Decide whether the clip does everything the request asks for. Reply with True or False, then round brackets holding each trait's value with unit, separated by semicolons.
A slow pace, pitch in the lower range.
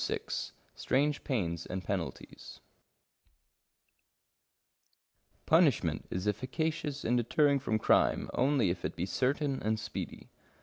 True (105 wpm; 120 Hz)